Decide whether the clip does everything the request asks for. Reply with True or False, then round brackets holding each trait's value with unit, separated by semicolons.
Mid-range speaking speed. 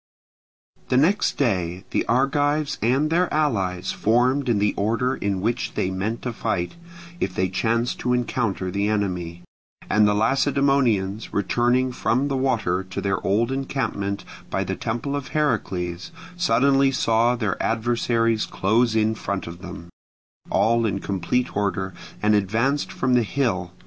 True (150 wpm)